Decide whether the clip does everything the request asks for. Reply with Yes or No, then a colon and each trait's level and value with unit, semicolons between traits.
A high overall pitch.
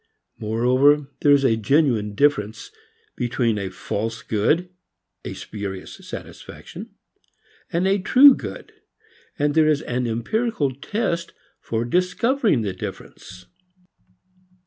No: low, 135 Hz